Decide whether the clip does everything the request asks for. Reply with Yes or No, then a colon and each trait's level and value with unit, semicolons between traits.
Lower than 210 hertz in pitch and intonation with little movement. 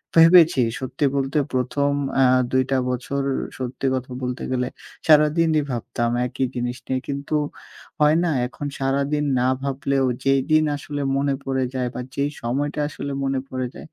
Yes: low, 135 Hz; narrow, 2.1 semitones